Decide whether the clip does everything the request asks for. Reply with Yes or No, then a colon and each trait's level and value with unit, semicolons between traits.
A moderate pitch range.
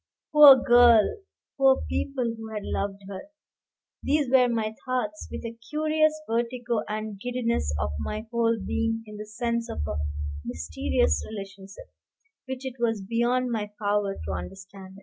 Yes: average, 3.6 semitones